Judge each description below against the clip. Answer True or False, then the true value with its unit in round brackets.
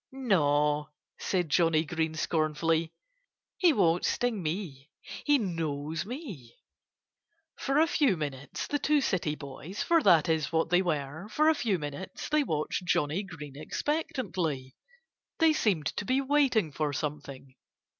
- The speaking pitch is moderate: True (165 Hz)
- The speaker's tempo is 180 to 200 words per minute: False (140 wpm)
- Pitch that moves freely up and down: True (7.5 semitones)